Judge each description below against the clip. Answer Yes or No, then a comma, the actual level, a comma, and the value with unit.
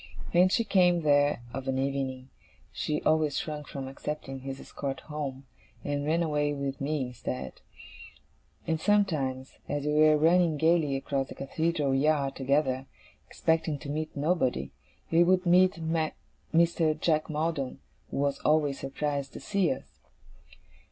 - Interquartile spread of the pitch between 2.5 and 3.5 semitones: Yes, average, 3.0 semitones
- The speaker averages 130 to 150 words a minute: Yes, average, 145 wpm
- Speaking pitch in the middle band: Yes, medium, 150 Hz